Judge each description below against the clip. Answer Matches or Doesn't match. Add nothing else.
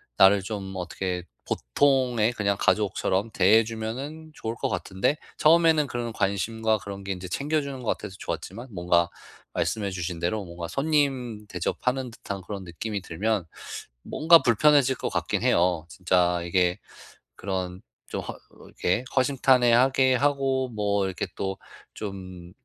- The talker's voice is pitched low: Matches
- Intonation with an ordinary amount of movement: Doesn't match